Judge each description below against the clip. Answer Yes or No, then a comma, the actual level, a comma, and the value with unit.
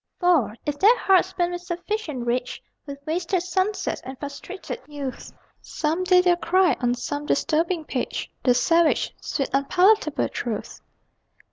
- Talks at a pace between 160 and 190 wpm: No, average, 140 wpm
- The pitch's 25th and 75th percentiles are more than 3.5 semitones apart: Yes, average, 4.7 semitones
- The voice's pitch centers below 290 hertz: No, very high, 330 Hz